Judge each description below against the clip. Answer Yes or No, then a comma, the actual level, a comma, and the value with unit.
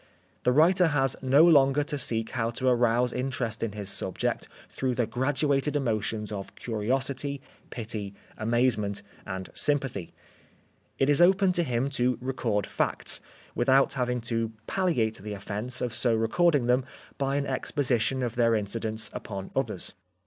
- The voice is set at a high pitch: No, low, 125 Hz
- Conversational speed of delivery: Yes, average, 150 wpm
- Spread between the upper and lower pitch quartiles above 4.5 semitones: No, average, 3.5 semitones